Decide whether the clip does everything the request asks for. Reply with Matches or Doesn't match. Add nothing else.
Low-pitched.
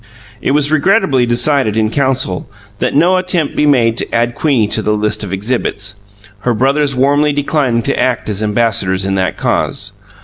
Matches